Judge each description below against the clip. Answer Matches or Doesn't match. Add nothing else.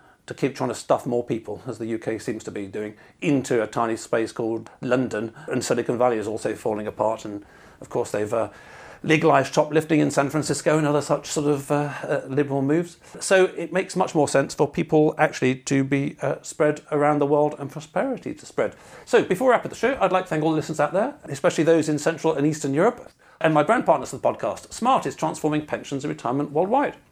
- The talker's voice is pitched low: Doesn't match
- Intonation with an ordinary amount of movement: Matches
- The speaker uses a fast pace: Matches